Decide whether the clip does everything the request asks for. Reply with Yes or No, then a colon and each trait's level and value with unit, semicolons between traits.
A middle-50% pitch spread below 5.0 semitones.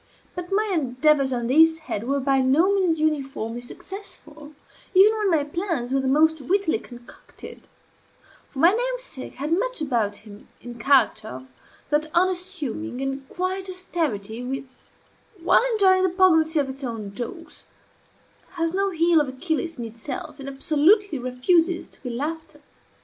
No: wide, 5.6 semitones